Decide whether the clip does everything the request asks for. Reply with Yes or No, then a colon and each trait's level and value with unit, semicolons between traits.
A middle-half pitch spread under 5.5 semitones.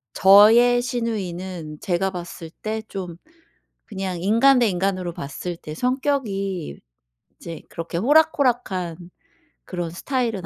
Yes: average, 5.1 semitones